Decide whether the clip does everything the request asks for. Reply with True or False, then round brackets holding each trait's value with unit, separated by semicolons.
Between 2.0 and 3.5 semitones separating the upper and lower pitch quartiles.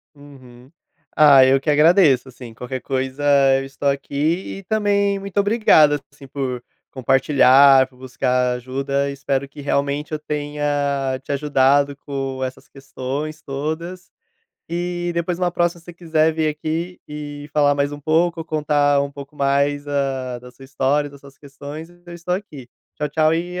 True (2.8 semitones)